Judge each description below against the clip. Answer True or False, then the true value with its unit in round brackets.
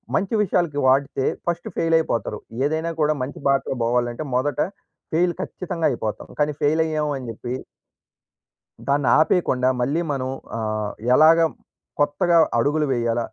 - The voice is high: False (145 Hz)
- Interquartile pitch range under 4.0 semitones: False (4.3 semitones)